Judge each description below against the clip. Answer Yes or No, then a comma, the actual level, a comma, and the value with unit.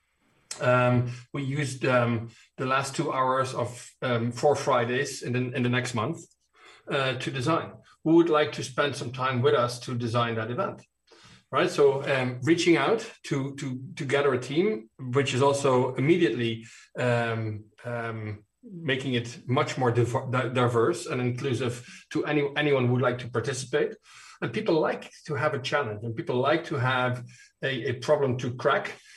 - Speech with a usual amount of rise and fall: Yes, average, 3.0 semitones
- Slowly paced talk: No, average, 175 wpm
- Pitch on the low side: Yes, low, 130 Hz